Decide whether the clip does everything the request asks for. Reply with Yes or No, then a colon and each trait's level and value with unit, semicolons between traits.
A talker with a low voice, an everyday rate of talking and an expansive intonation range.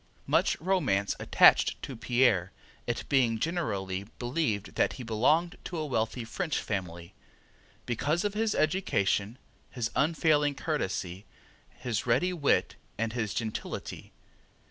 No: low, 125 Hz; slow, 120 wpm; wide, 6.6 semitones